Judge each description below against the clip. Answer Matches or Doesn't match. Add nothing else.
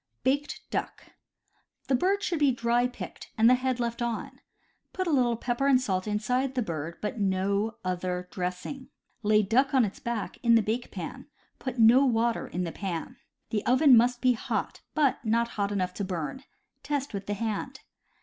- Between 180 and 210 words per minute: Matches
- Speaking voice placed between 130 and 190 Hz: Doesn't match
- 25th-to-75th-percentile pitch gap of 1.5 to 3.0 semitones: Doesn't match